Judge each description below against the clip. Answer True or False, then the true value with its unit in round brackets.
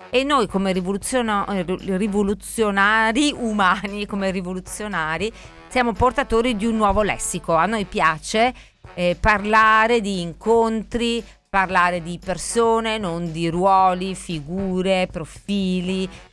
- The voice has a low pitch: False (195 Hz)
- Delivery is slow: True (105 wpm)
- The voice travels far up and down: False (3.4 semitones)